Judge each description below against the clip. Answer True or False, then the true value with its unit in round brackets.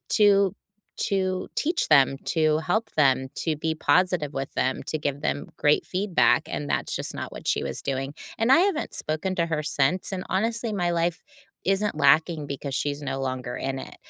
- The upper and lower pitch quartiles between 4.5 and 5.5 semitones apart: True (5.1 semitones)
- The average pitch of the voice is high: False (160 Hz)